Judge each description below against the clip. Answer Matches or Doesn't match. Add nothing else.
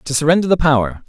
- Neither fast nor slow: Doesn't match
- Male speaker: Matches